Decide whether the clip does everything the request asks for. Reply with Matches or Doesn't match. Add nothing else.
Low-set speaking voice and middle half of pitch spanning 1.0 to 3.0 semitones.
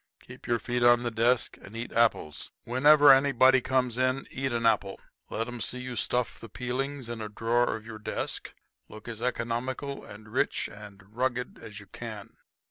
Matches